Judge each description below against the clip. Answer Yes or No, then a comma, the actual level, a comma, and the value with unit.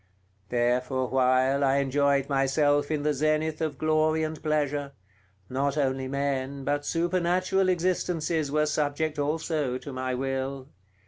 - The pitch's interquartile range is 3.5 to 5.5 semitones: No, narrow, 2.6 semitones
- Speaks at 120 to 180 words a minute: Yes, average, 140 wpm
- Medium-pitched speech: Yes, medium, 145 Hz